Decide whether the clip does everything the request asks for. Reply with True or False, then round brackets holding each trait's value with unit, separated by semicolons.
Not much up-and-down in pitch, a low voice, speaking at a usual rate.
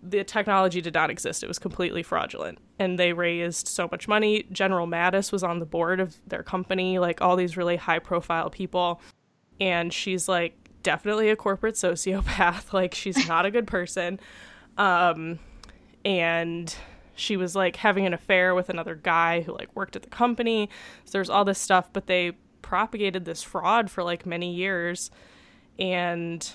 False (2.3 semitones; 180 Hz; 170 wpm)